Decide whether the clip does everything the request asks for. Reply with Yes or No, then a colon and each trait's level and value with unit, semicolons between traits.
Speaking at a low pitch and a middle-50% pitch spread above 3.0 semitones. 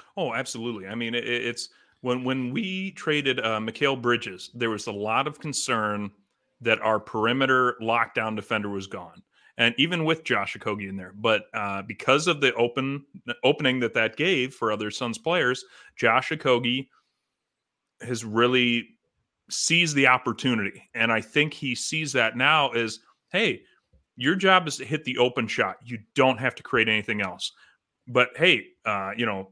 Yes: low, 120 Hz; average, 3.4 semitones